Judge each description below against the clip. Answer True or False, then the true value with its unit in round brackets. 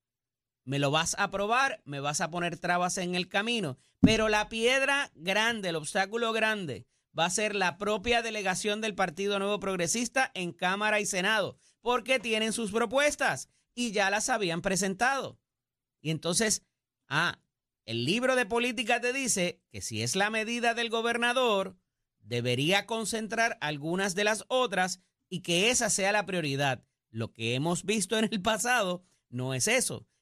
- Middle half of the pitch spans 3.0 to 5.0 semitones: False (5.4 semitones)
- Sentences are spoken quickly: False (160 wpm)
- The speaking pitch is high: True (200 Hz)